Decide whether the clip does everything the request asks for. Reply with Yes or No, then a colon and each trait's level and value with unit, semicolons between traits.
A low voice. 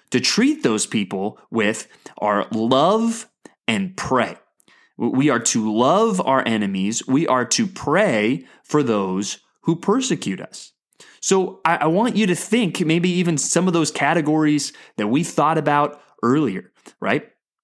No: medium, 165 Hz